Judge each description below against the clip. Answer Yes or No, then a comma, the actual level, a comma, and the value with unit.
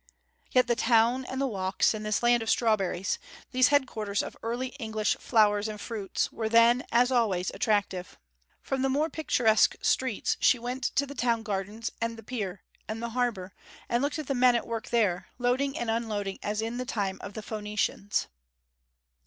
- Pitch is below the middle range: No, high, 230 Hz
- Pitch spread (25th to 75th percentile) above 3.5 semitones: No, average, 3.1 semitones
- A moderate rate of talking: Yes, average, 185 wpm